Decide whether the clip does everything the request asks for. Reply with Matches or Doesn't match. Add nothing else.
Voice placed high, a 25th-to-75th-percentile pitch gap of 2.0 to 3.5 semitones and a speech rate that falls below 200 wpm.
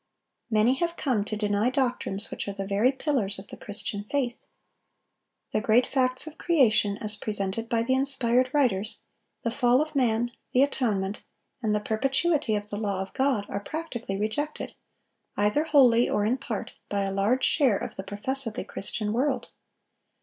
Doesn't match